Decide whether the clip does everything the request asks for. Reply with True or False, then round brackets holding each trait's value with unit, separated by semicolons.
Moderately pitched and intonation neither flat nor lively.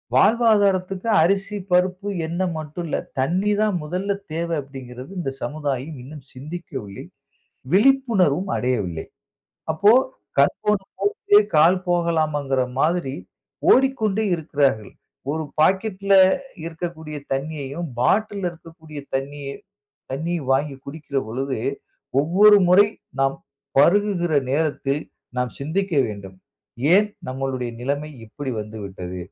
False (160 Hz; 5.9 semitones)